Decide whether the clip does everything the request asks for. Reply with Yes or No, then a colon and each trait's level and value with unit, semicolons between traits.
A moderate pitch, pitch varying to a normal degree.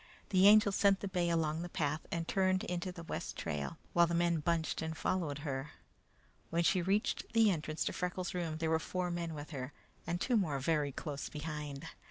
Yes: medium, 170 Hz; average, 3.1 semitones